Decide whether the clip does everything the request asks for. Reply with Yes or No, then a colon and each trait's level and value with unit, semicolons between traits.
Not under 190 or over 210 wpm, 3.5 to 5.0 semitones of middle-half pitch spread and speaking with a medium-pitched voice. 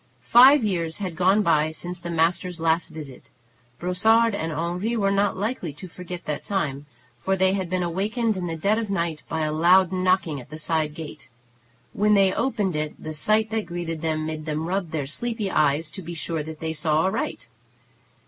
Yes: average, 195 wpm; average, 3.9 semitones; medium, 175 Hz